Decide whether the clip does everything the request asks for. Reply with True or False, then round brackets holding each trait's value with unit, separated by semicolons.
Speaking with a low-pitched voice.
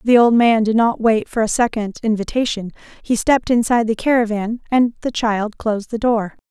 False (225 Hz)